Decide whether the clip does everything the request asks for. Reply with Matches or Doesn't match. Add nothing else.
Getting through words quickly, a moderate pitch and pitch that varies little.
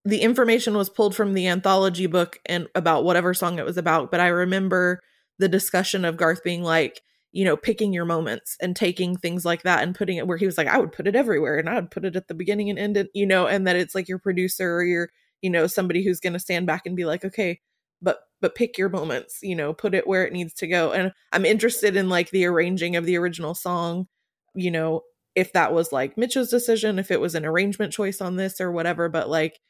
Matches